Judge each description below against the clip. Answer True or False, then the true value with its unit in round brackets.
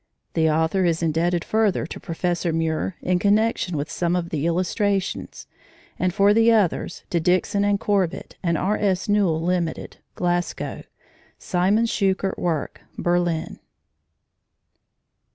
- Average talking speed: False (125 wpm)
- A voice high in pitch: False (180 Hz)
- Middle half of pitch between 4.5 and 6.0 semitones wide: False (3.1 semitones)